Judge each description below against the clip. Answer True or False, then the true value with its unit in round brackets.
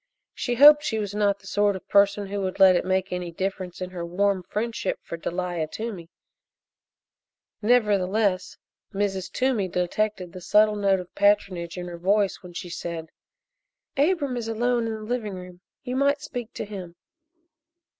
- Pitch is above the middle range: True (200 Hz)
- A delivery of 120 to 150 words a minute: False (165 wpm)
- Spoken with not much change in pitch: False (3.2 semitones)